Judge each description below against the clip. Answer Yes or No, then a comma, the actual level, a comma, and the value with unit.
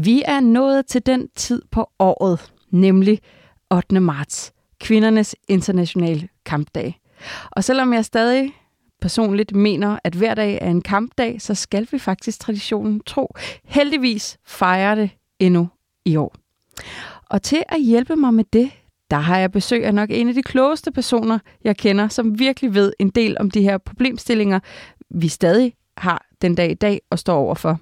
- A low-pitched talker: No, high, 210 Hz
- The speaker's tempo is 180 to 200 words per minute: No, average, 165 wpm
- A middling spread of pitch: Yes, average, 4.4 semitones